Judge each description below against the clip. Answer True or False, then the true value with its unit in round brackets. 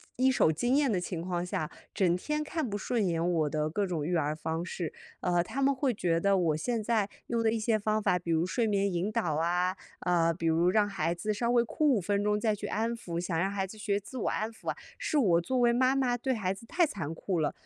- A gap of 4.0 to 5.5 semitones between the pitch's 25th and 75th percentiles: True (5.2 semitones)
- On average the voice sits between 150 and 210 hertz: True (200 Hz)